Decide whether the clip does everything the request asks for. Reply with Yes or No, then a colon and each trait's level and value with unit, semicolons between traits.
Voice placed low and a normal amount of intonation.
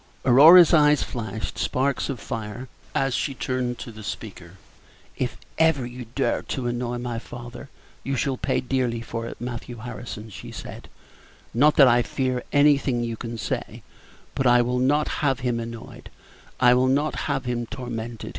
No: low, 125 Hz; narrow, 2.3 semitones